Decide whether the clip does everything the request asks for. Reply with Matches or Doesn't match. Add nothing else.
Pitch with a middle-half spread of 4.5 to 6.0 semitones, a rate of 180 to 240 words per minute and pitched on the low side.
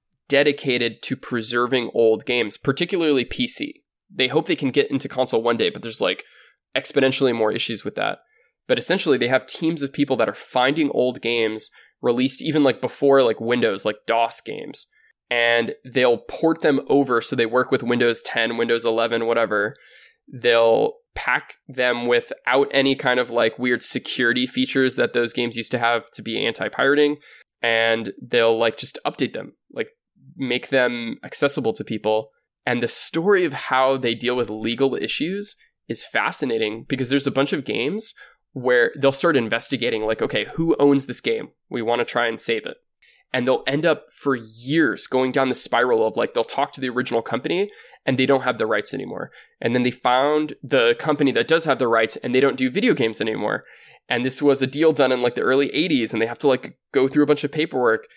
Doesn't match